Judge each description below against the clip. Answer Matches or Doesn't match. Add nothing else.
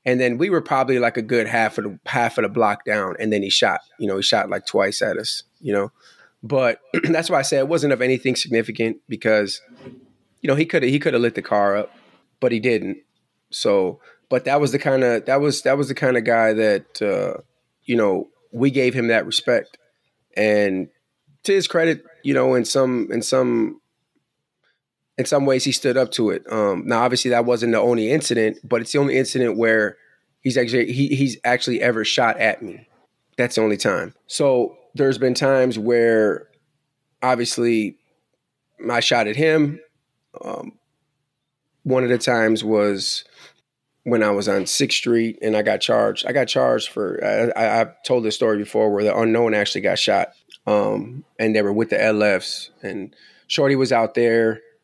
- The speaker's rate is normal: Matches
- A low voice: Matches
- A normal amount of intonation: Matches